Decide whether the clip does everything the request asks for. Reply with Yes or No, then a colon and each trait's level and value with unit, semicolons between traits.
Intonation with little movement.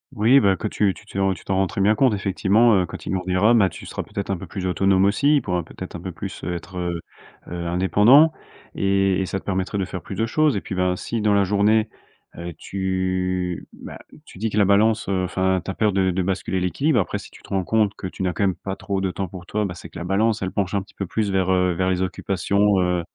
Yes: narrow, 2.0 semitones